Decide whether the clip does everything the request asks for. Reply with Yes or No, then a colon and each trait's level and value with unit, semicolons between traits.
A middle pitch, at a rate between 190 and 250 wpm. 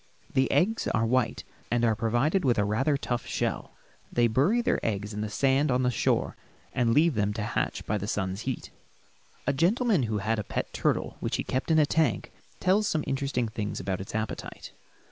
No: low, 120 Hz; average, 200 wpm